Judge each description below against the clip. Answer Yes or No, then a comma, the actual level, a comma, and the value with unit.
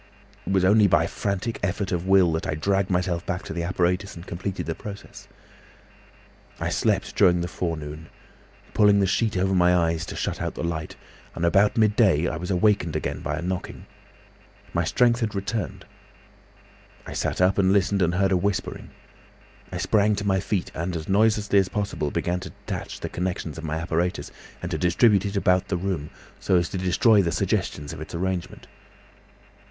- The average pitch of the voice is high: No, very low, 90 Hz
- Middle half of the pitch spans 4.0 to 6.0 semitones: No, average, 2.8 semitones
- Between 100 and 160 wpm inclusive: No, average, 190 wpm